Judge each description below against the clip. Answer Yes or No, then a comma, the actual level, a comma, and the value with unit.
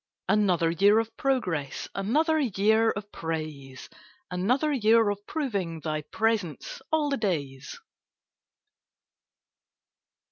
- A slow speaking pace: Yes, slow, 100 wpm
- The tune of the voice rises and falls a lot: Yes, wide, 5.9 semitones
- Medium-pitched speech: No, high, 205 Hz